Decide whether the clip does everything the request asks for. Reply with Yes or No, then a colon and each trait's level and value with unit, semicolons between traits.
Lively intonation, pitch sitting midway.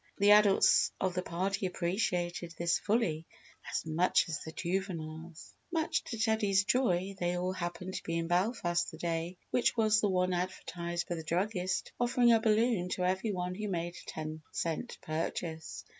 No: average, 3.3 semitones; medium, 180 Hz